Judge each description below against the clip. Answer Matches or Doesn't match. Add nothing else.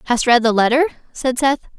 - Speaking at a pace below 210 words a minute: Matches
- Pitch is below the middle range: Doesn't match